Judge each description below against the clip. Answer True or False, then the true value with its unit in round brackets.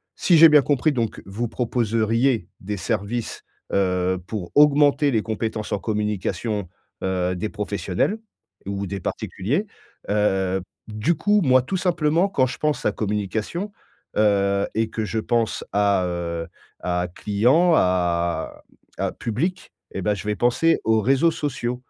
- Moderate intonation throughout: False (5.7 semitones)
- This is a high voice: False (110 Hz)